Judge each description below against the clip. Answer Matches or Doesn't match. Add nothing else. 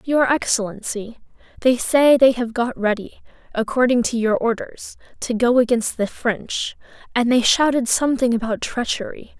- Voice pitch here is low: Doesn't match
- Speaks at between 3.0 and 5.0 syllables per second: Matches